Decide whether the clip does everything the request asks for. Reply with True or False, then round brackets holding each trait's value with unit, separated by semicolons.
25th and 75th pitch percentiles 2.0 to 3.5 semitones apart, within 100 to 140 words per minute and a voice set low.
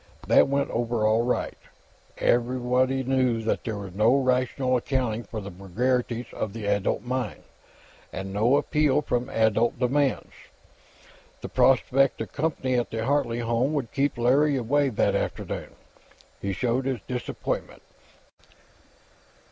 True (2.9 semitones; 135 wpm; 125 Hz)